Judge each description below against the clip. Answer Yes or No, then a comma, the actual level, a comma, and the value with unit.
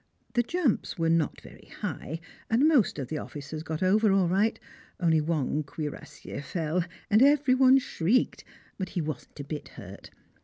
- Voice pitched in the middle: Yes, medium, 175 Hz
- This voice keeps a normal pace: Yes, average, 165 wpm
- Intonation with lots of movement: Yes, wide, 6.9 semitones